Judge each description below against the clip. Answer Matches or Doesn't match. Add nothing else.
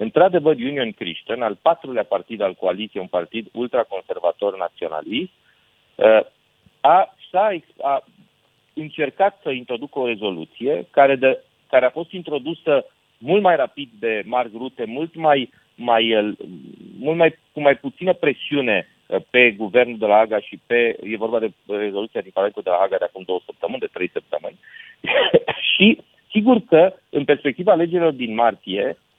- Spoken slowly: Doesn't match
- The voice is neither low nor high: Matches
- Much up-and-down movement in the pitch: Matches